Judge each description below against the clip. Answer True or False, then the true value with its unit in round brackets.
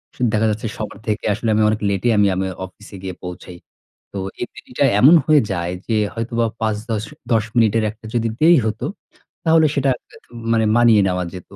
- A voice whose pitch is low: True (110 Hz)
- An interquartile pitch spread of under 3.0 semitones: True (2.6 semitones)